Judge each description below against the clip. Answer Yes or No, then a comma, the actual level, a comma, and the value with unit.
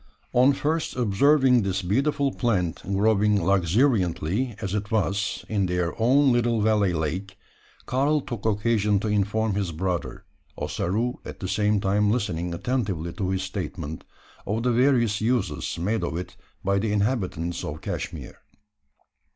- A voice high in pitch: No, low, 105 Hz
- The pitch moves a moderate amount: Yes, average, 4.1 semitones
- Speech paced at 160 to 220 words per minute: No, average, 145 wpm